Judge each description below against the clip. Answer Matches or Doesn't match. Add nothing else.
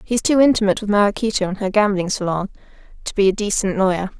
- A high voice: Matches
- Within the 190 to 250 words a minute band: Matches